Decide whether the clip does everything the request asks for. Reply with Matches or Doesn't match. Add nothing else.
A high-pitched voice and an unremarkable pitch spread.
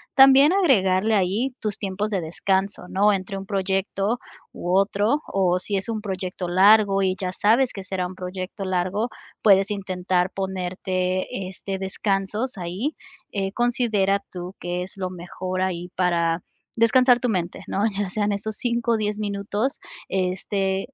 Doesn't match